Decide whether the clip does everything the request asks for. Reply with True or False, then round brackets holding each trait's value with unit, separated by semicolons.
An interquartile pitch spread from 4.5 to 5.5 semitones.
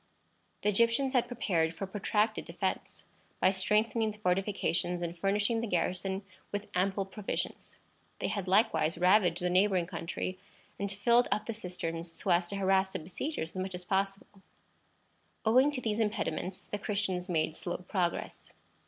False (2.9 semitones)